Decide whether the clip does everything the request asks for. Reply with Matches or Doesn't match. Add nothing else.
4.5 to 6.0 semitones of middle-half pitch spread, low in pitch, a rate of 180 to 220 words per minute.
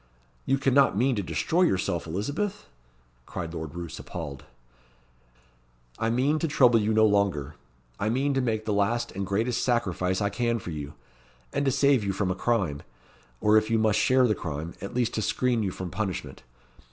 Matches